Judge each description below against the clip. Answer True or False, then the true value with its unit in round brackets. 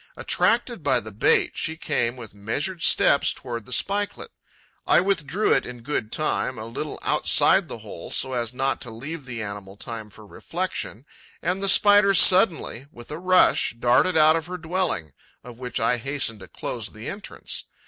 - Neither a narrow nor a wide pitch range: False (7.4 semitones)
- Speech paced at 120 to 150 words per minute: False (180 wpm)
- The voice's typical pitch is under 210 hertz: True (135 Hz)